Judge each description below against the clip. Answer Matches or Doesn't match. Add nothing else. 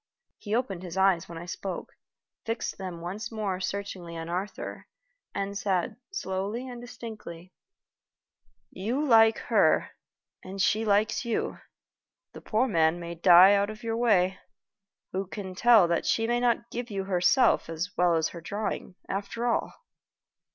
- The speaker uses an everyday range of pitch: Matches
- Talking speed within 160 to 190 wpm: Doesn't match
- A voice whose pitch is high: Matches